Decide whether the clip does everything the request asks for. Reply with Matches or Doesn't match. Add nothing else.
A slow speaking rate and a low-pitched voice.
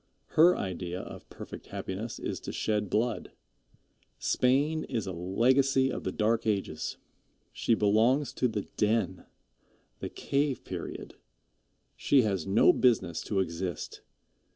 Matches